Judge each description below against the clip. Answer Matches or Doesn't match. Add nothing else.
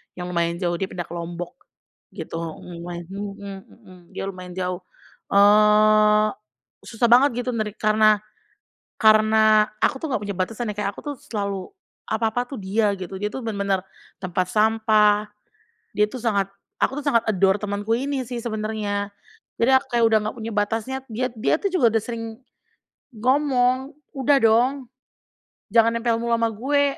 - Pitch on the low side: Doesn't match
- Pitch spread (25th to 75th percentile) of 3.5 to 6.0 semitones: Doesn't match